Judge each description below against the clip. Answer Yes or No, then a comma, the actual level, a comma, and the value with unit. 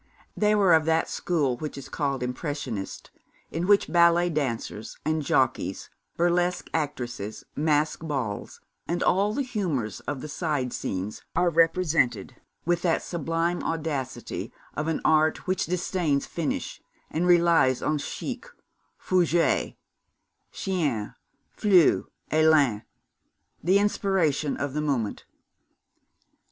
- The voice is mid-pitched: Yes, medium, 160 Hz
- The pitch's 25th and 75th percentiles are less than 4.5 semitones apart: Yes, average, 4.0 semitones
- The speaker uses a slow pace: Yes, slow, 120 wpm